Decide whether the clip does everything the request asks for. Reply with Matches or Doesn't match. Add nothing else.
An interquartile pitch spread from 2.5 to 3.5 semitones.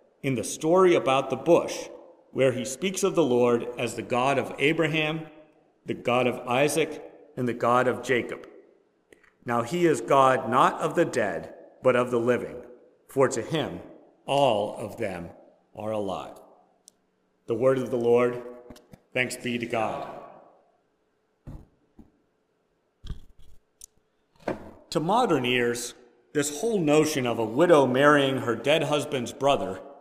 Doesn't match